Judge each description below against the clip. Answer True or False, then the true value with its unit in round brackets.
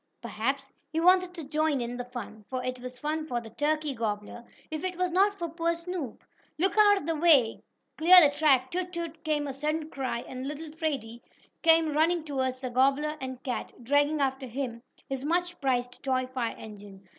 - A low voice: False (285 Hz)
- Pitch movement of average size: True (4.3 semitones)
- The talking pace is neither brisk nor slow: True (190 wpm)